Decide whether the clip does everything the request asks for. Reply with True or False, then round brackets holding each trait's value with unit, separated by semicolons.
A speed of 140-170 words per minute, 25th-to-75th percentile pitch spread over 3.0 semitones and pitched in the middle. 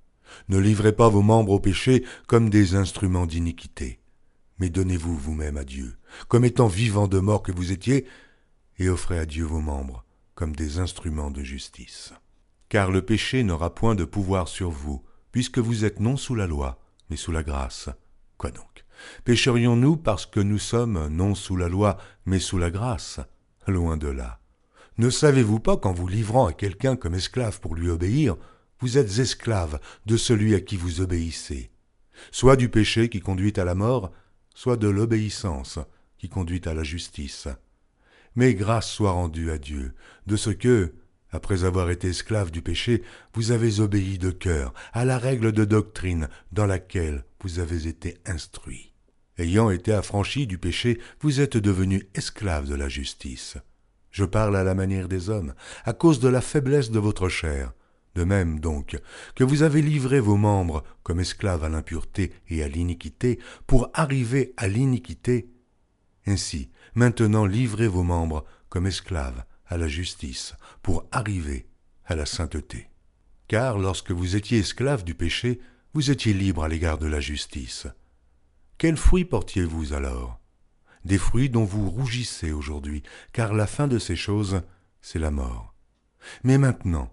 False (165 wpm; 5.4 semitones; 95 Hz)